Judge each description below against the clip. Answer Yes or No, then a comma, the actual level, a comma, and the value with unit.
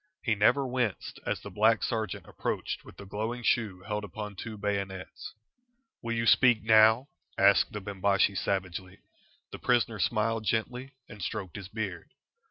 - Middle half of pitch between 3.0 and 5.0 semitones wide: No, narrow, 2.5 semitones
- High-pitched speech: No, low, 105 Hz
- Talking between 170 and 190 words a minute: No, average, 155 wpm